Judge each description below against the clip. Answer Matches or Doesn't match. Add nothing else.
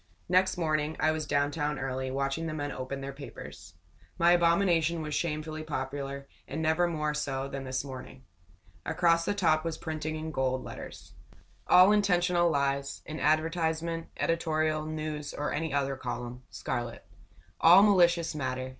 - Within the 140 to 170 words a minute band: Matches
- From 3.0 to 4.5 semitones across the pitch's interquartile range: Matches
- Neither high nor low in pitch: Matches